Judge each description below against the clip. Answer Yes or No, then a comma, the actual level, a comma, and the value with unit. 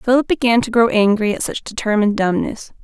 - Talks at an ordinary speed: Yes, average, 190 wpm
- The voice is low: No, high, 225 Hz